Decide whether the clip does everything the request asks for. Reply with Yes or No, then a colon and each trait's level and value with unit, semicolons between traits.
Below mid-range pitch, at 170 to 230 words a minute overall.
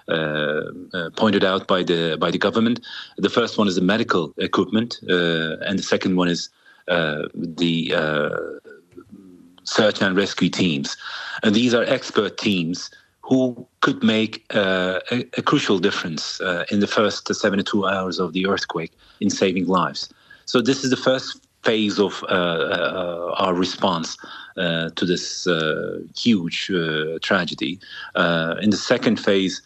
No: very low, 95 Hz; average, 155 wpm